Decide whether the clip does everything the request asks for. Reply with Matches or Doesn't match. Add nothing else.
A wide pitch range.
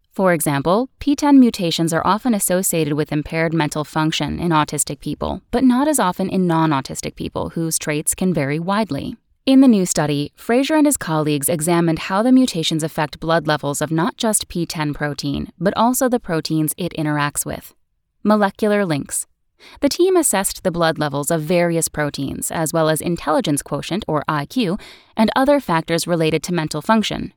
Matches